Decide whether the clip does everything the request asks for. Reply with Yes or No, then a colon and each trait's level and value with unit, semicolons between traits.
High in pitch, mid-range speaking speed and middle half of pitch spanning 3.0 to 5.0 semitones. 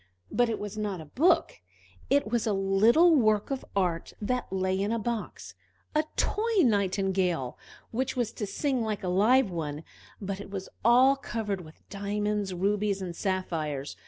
Yes: high, 205 Hz; average, 165 wpm; average, 4.0 semitones